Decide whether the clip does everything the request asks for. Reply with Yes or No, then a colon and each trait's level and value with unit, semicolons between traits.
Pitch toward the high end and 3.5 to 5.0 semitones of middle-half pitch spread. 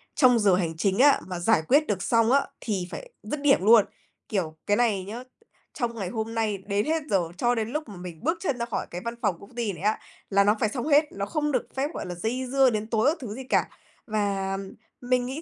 Yes: high, 225 Hz; average, 4.4 semitones